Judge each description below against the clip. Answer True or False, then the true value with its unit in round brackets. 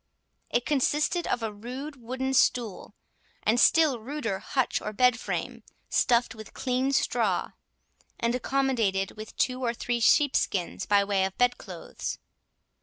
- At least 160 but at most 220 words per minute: False (140 wpm)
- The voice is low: False (245 Hz)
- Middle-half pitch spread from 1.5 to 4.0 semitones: True (3.5 semitones)